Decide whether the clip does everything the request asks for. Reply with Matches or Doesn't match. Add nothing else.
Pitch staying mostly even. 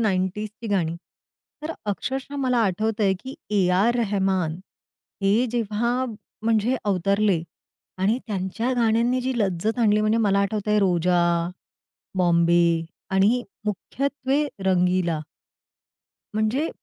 Doesn't match